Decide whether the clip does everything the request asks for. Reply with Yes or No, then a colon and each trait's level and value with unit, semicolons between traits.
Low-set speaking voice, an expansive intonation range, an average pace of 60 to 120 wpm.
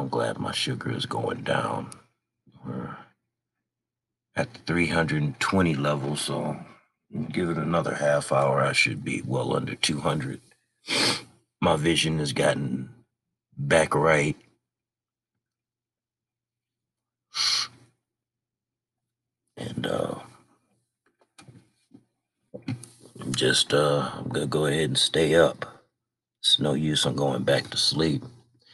Yes: low, 115 Hz; wide, 8.5 semitones; slow, 105 wpm